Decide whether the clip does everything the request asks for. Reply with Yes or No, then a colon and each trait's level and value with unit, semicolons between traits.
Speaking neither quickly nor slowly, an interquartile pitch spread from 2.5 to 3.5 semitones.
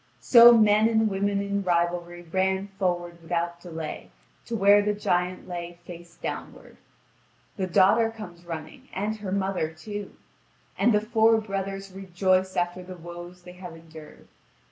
Yes: average, 145 wpm; average, 2.8 semitones